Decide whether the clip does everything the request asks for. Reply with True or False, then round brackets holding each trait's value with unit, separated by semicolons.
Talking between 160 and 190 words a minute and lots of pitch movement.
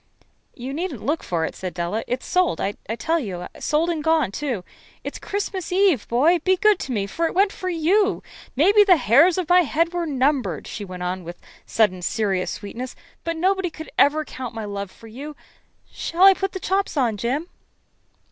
False (200 wpm; 8.5 semitones)